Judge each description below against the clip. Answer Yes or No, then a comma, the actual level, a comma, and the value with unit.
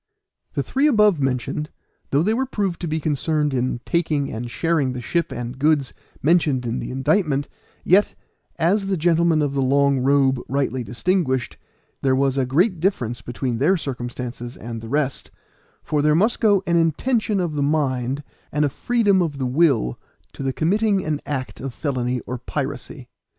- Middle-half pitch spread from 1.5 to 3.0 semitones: No, average, 4.7 semitones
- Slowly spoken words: No, average, 175 wpm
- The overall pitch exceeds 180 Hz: No, medium, 145 Hz